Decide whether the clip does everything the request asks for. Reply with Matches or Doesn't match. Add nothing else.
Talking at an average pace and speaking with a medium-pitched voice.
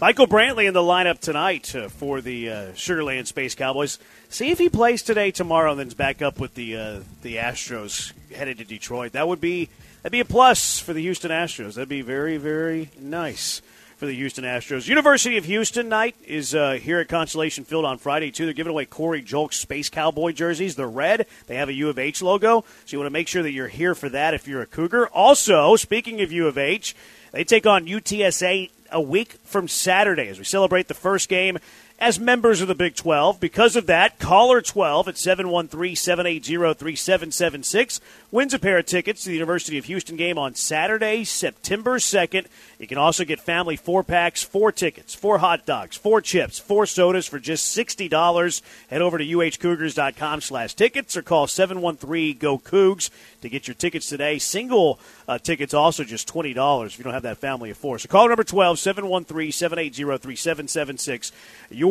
Doesn't match